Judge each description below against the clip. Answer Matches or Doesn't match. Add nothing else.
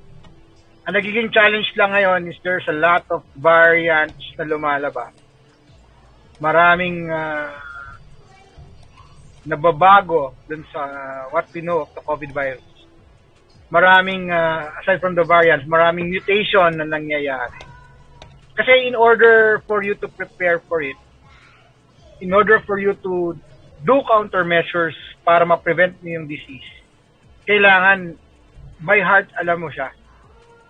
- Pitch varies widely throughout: Doesn't match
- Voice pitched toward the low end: Doesn't match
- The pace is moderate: Matches